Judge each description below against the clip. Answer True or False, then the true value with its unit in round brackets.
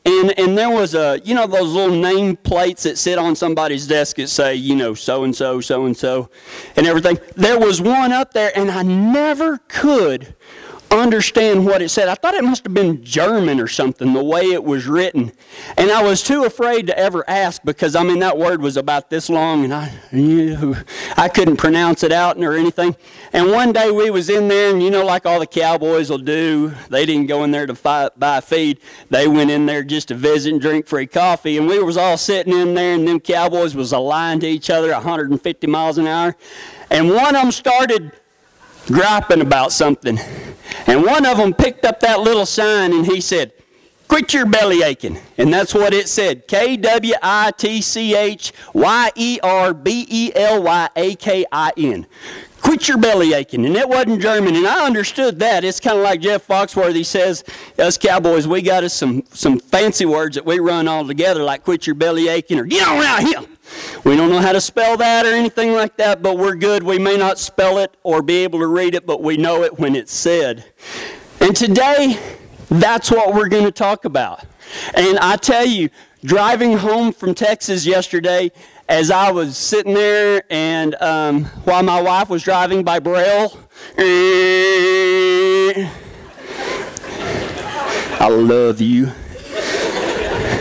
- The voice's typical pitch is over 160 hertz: True (185 Hz)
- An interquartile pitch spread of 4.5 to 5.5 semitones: True (4.8 semitones)